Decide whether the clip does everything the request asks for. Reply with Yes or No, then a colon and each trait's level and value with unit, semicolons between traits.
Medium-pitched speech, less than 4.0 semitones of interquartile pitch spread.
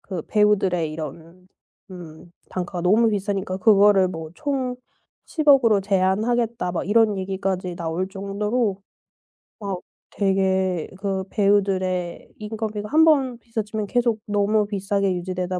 No: high, 195 Hz; average, 2.7 semitones